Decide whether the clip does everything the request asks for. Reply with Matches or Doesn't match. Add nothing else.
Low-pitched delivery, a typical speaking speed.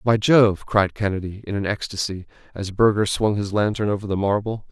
Matches